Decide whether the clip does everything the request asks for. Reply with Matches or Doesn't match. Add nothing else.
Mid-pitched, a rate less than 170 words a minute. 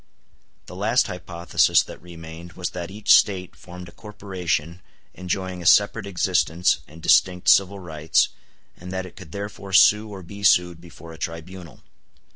Doesn't match